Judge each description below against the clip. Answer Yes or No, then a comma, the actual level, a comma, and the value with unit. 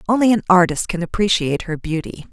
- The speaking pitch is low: No, medium, 185 Hz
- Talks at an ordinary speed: Yes, average, 180 wpm